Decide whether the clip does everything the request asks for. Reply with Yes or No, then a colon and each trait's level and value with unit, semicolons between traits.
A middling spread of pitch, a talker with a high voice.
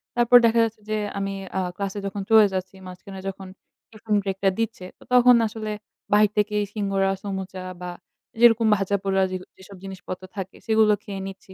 No: narrow, 2.2 semitones; high, 200 Hz